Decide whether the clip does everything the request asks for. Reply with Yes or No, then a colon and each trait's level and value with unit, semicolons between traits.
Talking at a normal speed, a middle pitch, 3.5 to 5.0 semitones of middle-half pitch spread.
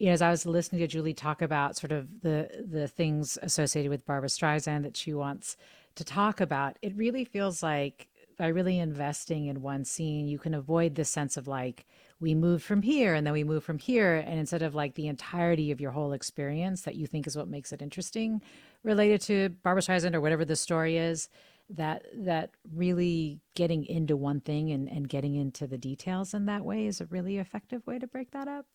No: fast, 215 wpm; medium, 160 Hz; average, 3.8 semitones